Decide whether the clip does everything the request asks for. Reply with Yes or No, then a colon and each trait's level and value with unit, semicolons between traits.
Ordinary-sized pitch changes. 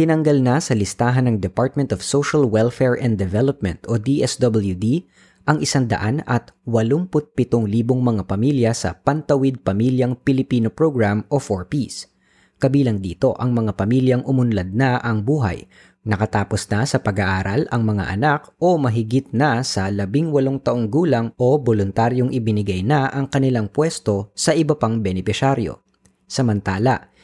Yes: average, 4.3 semitones